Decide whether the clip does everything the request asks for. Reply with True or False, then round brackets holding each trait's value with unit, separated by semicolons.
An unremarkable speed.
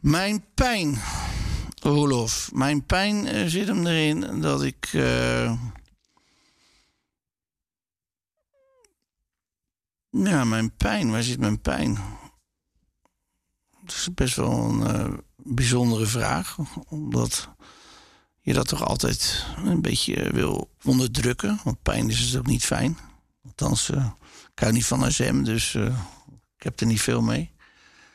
False (120 wpm)